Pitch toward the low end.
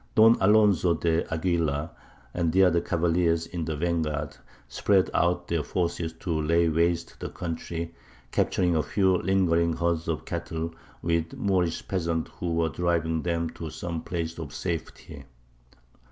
Yes: very low, 85 Hz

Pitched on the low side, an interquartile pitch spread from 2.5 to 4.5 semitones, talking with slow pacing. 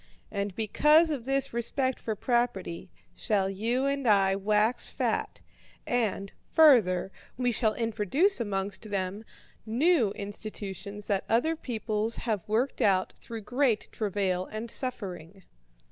No: high, 215 Hz; average, 3.7 semitones; slow, 125 wpm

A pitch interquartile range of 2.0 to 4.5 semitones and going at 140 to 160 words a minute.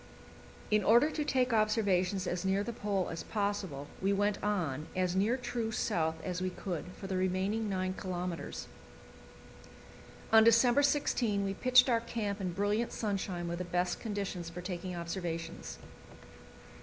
Yes: average, 3.5 semitones; average, 155 wpm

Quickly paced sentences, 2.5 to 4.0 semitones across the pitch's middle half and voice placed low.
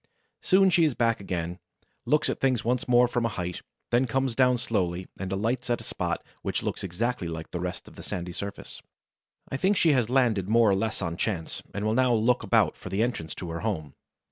No: fast, 220 wpm; average, 5.3 semitones; low, 115 Hz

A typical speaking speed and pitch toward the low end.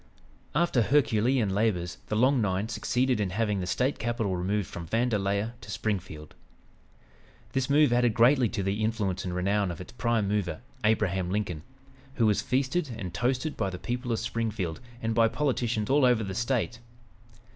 Yes: average, 170 wpm; low, 110 Hz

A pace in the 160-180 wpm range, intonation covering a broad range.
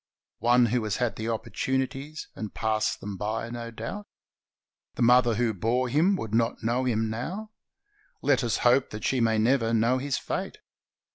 No: average, 165 wpm; narrow, 2.5 semitones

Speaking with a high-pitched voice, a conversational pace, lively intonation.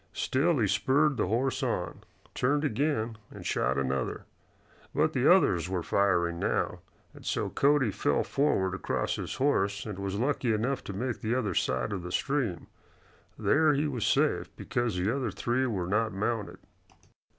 No: low, 110 Hz; average, 165 wpm; wide, 5.7 semitones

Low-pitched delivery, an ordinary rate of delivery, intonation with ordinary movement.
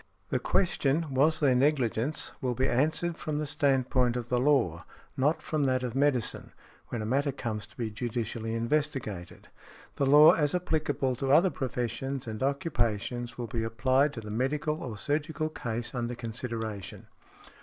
Yes: low, 130 Hz; average, 165 wpm; average, 3.9 semitones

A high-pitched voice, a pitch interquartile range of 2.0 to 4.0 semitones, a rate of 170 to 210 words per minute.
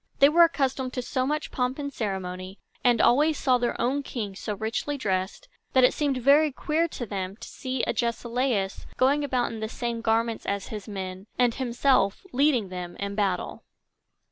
No: high, 240 Hz; average, 5.1 semitones; average, 180 wpm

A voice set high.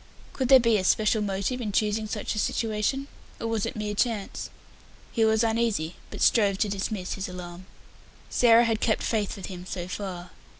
Yes: high, 210 Hz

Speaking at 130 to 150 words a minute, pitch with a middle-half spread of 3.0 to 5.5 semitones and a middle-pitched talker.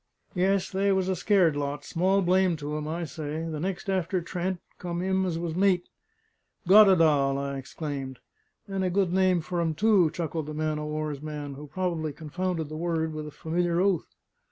No: average, 190 wpm; average, 3.5 semitones; medium, 170 Hz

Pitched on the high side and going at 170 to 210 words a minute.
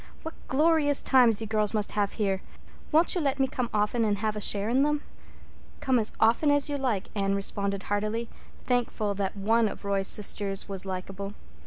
Yes: high, 215 Hz; average, 190 wpm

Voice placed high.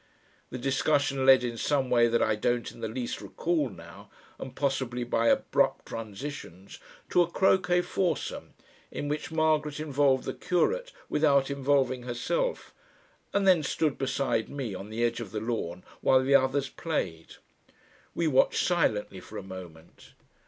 No: low, 130 Hz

